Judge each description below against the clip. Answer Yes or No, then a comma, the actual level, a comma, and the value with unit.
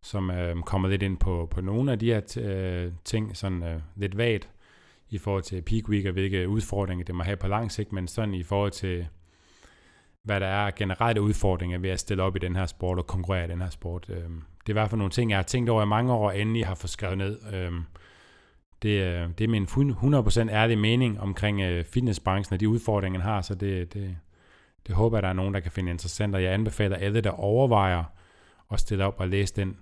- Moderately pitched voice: No, low, 100 Hz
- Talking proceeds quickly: Yes, fast, 235 wpm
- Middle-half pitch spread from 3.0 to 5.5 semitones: No, narrow, 2.6 semitones